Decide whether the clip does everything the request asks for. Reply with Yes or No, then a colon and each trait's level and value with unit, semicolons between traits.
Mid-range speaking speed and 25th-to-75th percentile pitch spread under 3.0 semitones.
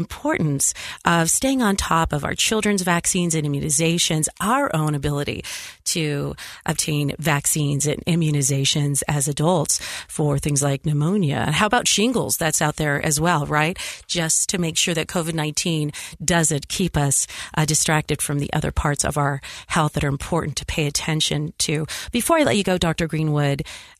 Yes: average, 165 wpm; narrow, 2.6 semitones